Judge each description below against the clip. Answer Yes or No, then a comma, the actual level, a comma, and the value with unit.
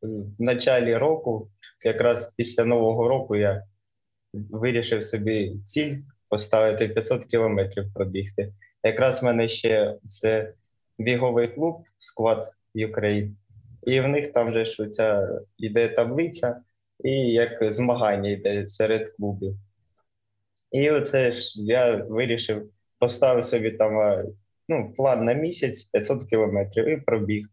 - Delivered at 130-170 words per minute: No, average, 115 wpm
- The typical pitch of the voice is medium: No, low, 110 Hz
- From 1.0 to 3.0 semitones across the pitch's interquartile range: Yes, average, 2.7 semitones